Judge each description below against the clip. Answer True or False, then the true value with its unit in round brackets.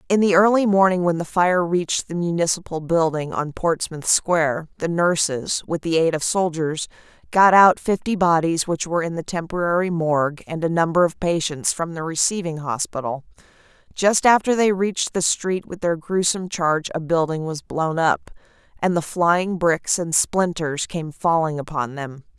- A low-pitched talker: False (170 Hz)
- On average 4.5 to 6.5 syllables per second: True (4.8 syllables/s)